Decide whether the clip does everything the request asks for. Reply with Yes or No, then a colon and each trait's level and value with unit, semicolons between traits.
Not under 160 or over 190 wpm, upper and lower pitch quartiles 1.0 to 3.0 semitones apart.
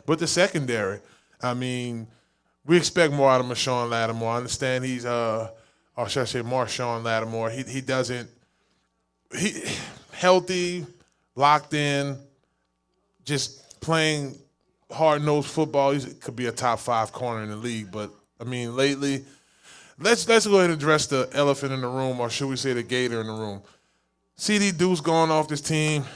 No: average, 170 wpm; average, 4.4 semitones